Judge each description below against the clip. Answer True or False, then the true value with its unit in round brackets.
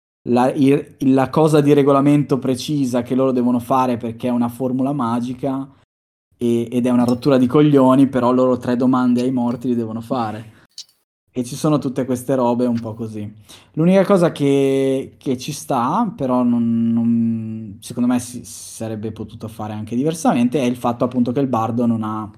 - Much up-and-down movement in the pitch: False (2.7 semitones)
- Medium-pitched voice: False (125 Hz)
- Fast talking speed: True (180 wpm)